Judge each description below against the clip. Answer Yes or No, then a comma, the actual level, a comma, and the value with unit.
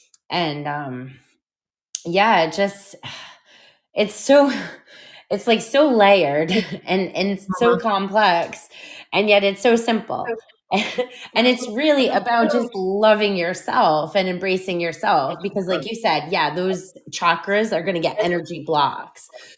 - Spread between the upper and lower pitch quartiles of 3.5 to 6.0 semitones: Yes, average, 4.3 semitones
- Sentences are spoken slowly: Yes, slow, 130 wpm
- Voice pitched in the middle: No, high, 200 Hz